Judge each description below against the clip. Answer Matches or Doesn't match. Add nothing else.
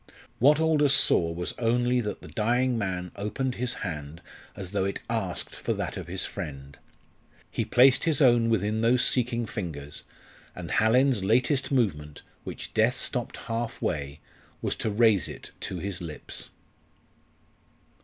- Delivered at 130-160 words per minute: Matches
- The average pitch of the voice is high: Doesn't match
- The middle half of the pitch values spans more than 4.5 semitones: Matches